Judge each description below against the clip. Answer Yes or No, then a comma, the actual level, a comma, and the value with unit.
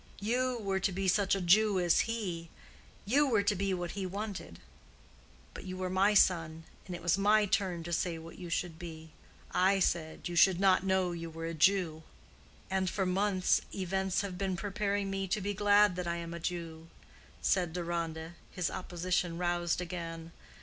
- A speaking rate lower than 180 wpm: No, average, 185 wpm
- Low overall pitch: No, medium, 185 Hz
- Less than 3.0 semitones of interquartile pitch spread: Yes, narrow, 2.5 semitones